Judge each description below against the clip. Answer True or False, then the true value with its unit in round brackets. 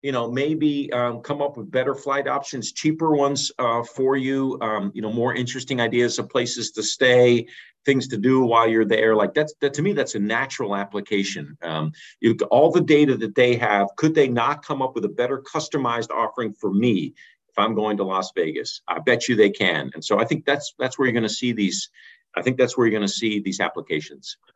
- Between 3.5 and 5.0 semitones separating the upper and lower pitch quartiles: True (4.4 semitones)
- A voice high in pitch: False (120 Hz)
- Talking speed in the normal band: False (230 wpm)